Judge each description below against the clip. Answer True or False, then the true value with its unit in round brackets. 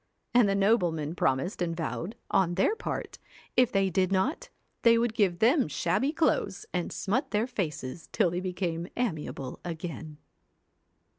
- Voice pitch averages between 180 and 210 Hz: True (190 Hz)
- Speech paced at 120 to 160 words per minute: True (150 wpm)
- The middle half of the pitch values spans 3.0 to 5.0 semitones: False (5.6 semitones)